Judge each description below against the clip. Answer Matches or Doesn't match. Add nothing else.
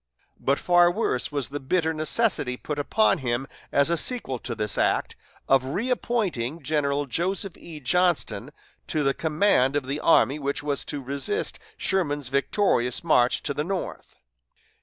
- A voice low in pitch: Doesn't match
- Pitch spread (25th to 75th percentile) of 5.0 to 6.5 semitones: Doesn't match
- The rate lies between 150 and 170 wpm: Matches